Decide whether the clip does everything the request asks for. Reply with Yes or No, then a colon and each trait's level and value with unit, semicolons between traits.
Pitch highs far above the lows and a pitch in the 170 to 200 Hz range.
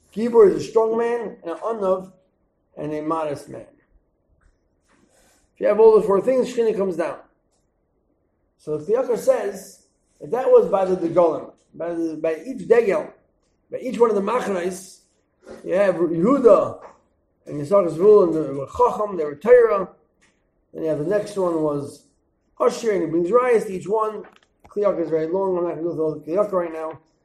Yes: wide, 5.7 semitones; medium, 185 Hz